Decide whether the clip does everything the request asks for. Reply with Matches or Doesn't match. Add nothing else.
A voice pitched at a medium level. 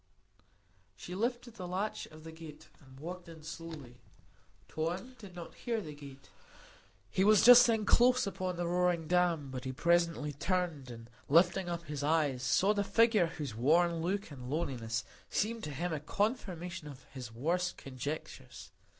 Matches